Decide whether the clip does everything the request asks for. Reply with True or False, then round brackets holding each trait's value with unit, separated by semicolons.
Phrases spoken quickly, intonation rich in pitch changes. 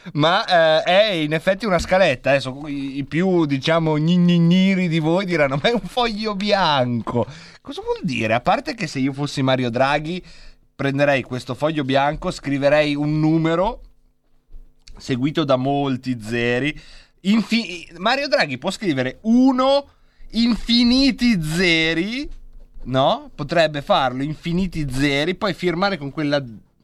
False (130 wpm; 5.9 semitones)